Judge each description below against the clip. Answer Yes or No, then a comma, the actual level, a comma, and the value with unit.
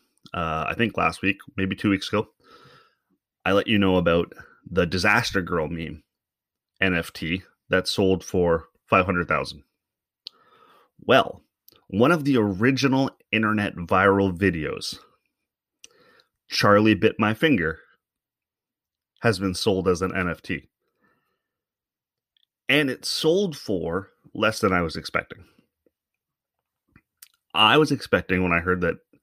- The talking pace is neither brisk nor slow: No, slow, 120 wpm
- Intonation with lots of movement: No, average, 3.2 semitones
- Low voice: Yes, low, 100 Hz